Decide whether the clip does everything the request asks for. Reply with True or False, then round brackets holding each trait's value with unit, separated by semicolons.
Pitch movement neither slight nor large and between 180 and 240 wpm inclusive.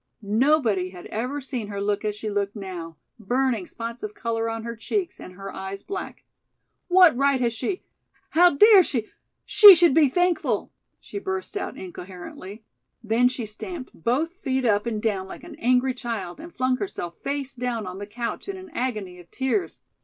False (6.1 semitones; 185 wpm)